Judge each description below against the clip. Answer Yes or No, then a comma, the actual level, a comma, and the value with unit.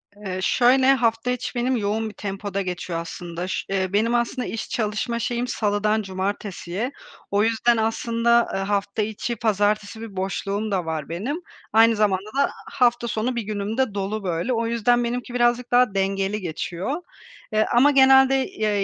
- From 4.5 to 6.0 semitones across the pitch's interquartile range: No, average, 3.4 semitones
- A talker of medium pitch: No, high, 215 Hz